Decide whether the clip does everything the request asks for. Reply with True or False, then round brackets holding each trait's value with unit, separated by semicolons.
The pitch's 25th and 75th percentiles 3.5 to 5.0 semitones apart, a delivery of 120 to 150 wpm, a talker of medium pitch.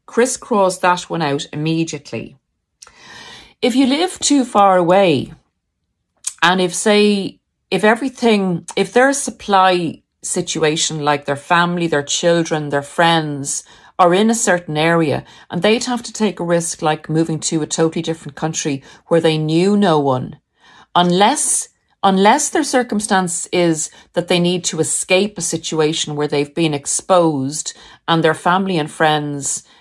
True (4.4 semitones; 145 wpm; 175 Hz)